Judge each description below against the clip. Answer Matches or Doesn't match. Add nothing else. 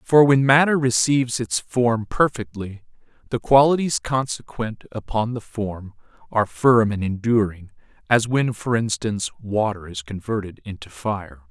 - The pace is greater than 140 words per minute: Doesn't match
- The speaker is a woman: Doesn't match